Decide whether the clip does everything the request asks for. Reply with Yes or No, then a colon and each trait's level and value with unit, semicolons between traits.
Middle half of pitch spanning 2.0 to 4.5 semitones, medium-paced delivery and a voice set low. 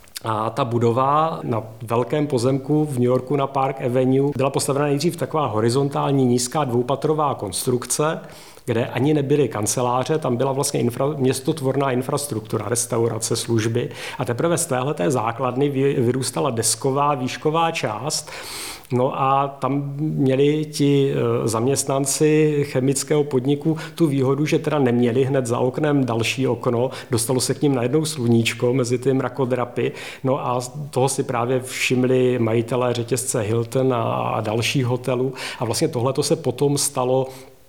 Yes: narrow, 2.6 semitones; average, 135 wpm; low, 130 Hz